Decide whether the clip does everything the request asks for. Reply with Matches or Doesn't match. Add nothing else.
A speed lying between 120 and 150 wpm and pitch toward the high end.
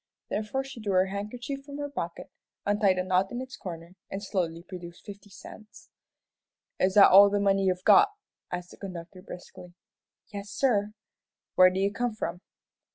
Doesn't match